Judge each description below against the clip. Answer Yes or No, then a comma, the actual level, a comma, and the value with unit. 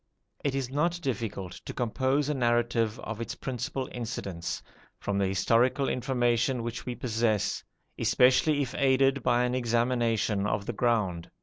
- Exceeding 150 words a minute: No, average, 145 wpm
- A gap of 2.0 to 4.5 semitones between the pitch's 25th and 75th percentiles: Yes, average, 2.8 semitones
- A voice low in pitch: Yes, low, 120 Hz